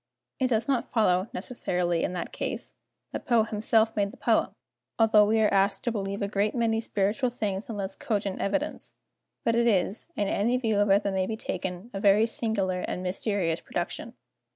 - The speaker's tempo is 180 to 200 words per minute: Yes, average, 195 wpm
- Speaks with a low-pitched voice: No, high, 205 Hz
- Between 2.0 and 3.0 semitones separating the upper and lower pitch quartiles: Yes, narrow, 2.6 semitones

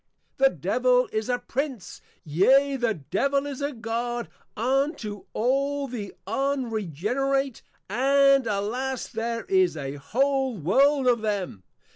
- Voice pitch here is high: Yes, very high, 250 Hz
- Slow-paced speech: Yes, slow, 125 wpm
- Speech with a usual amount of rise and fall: Yes, average, 4.3 semitones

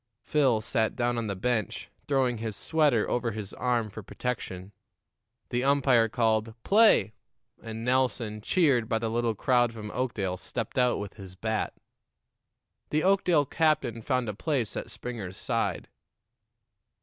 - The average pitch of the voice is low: Yes, low, 115 Hz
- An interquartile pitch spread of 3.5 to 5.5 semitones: No, average, 3.0 semitones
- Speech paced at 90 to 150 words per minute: Yes, average, 145 wpm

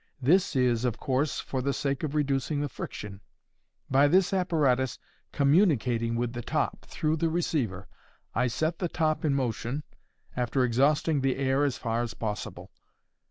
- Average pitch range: Yes, average, 4.0 semitones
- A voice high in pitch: No, low, 135 Hz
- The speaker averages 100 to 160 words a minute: Yes, average, 155 wpm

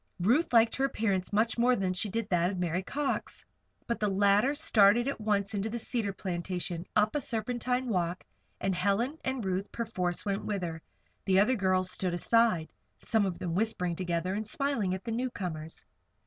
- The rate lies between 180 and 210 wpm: Yes, average, 185 wpm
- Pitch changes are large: No, average, 4.1 semitones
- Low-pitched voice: No, high, 200 Hz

